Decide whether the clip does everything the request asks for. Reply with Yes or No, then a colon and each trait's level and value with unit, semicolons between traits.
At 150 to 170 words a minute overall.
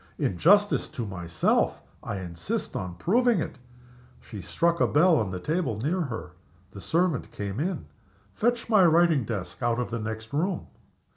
Yes: average, 165 wpm